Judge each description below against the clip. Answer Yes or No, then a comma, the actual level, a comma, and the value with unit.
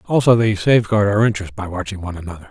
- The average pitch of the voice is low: Yes, low, 100 Hz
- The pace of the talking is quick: Yes, fast, 215 wpm